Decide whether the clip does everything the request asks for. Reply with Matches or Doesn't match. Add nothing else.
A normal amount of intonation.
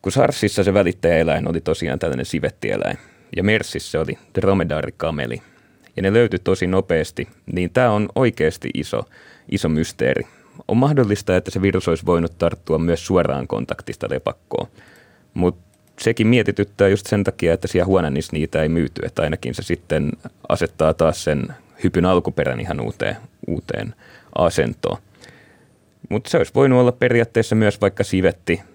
Matches